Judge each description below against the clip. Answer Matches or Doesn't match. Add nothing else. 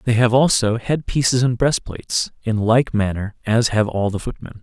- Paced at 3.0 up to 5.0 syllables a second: Matches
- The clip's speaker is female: Doesn't match